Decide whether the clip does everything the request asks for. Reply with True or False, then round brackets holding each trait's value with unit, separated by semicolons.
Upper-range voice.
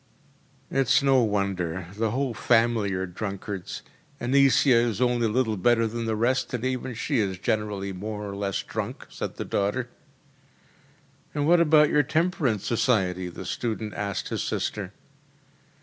False (115 Hz)